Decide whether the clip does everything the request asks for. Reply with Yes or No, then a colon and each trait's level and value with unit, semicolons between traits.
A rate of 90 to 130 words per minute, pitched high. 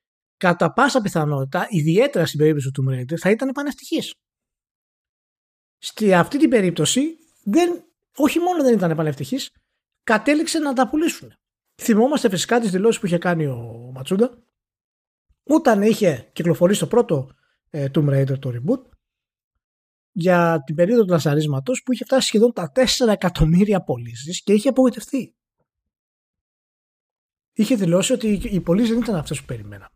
No: average, 140 wpm; high, 200 Hz